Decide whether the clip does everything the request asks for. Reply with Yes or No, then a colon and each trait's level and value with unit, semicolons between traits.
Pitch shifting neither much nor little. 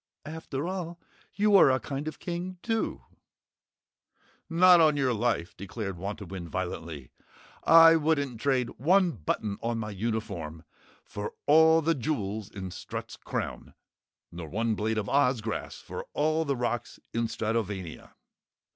No: wide, 7.6 semitones